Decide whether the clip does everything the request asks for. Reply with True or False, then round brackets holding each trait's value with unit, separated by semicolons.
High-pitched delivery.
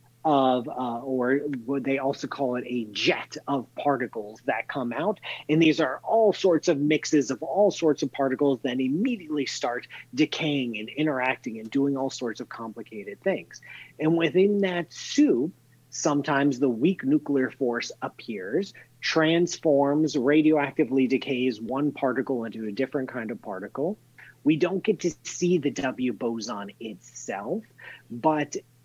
False (140 Hz)